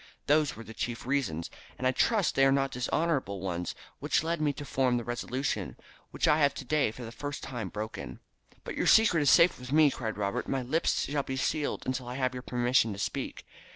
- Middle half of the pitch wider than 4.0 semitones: No, average, 3.3 semitones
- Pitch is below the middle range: Yes, low, 130 Hz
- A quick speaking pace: Yes, fast, 220 wpm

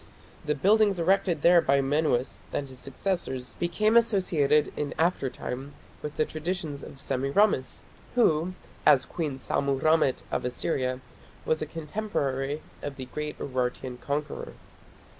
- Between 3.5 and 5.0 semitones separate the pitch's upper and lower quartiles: Yes, average, 4.1 semitones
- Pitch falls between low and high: Yes, medium, 150 Hz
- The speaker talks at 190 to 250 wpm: No, slow, 135 wpm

